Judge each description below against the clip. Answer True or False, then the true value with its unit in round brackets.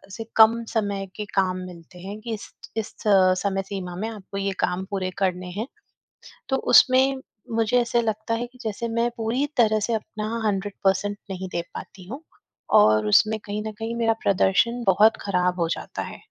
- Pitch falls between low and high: False (210 Hz)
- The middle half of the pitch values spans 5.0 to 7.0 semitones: False (3.1 semitones)